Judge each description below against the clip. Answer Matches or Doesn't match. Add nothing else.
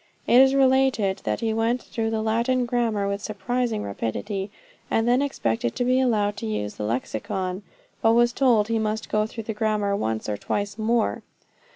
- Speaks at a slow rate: Doesn't match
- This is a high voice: Matches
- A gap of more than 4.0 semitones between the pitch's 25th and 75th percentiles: Doesn't match